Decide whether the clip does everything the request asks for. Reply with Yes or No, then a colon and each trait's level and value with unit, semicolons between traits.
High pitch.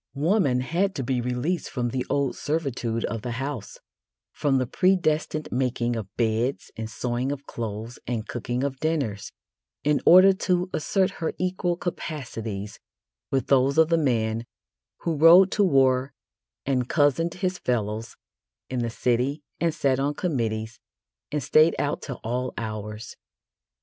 No: low, 135 Hz